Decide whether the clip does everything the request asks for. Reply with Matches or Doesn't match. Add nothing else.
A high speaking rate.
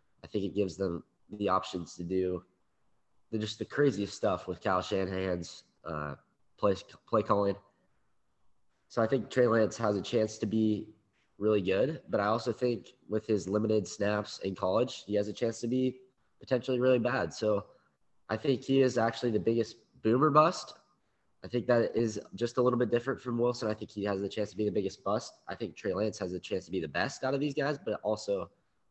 Matches